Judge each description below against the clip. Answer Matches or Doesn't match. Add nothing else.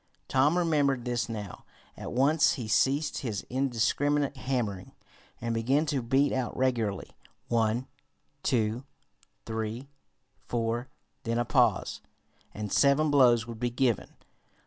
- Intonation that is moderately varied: Matches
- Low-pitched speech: Matches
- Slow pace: Matches